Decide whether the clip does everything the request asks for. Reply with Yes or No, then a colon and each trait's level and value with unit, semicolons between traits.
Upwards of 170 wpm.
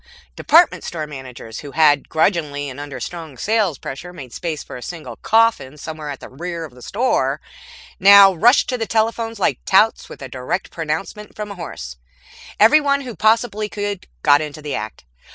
Yes: average, 180 wpm